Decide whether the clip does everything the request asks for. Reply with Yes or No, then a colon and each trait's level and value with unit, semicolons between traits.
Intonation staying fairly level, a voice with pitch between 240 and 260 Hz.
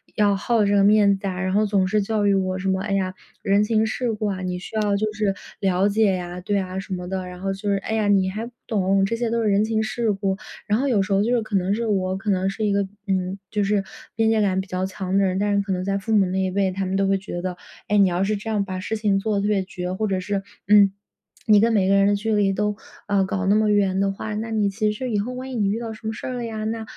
No: narrow, 2.1 semitones; high, 200 Hz